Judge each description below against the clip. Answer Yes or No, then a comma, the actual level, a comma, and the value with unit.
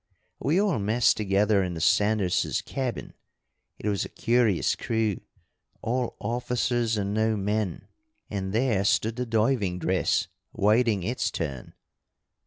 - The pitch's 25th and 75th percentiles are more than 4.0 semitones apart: No, average, 3.2 semitones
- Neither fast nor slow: No, slow, 130 wpm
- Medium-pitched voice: No, low, 110 Hz